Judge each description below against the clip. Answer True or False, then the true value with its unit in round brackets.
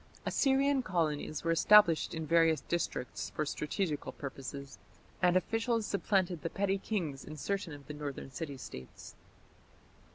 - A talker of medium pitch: True (165 Hz)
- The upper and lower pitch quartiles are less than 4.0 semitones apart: False (5.1 semitones)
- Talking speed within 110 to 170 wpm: True (135 wpm)